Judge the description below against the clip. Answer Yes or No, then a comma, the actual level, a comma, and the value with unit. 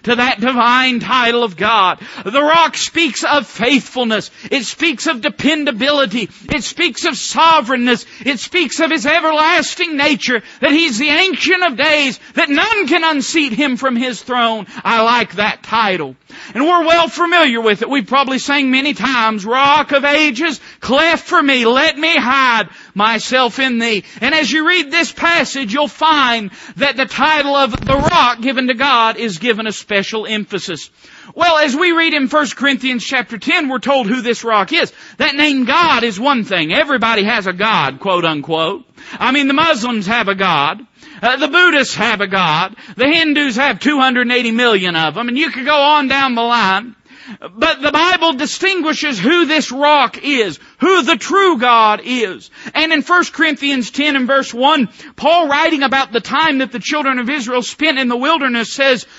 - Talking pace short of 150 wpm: No, average, 180 wpm